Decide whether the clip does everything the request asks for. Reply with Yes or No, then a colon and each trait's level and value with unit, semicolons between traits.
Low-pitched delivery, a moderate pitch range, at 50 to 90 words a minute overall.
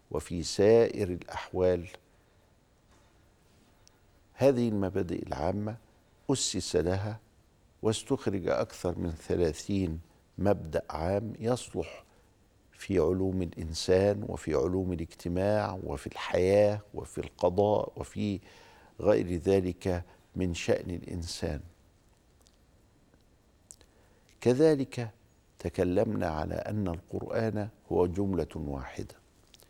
Yes: very low, 95 Hz; average, 3.1 semitones; average, 80 wpm